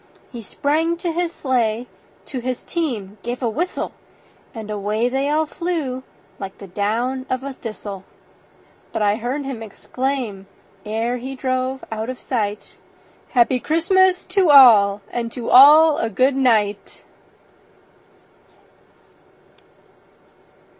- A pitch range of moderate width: Yes, average, 4.5 semitones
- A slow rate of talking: Yes, slow, 125 wpm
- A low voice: No, very high, 250 Hz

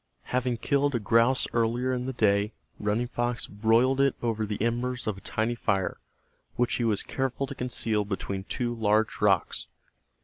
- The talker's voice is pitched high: No, low, 115 Hz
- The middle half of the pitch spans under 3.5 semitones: Yes, average, 2.9 semitones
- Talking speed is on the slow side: No, average, 170 wpm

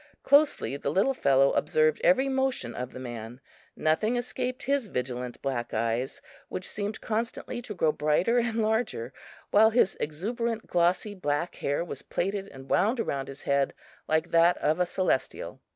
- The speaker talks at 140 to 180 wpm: Yes, average, 160 wpm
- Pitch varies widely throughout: Yes, wide, 8.6 semitones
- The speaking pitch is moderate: Yes, medium, 175 Hz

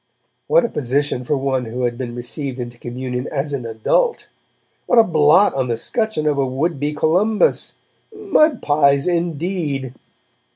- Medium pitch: Yes, medium, 145 Hz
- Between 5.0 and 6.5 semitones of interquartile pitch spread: Yes, wide, 5.4 semitones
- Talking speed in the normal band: Yes, average, 160 wpm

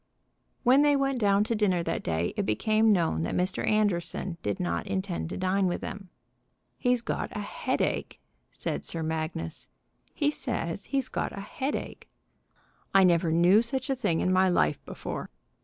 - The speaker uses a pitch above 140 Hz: Yes, high, 190 Hz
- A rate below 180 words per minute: Yes, average, 170 wpm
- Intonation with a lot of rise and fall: Yes, wide, 5.9 semitones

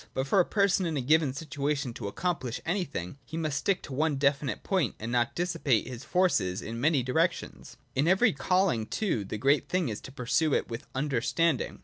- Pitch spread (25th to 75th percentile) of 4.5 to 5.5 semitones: Yes, average, 5.2 semitones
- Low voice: No, medium, 145 Hz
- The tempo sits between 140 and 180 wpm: No, average, 200 wpm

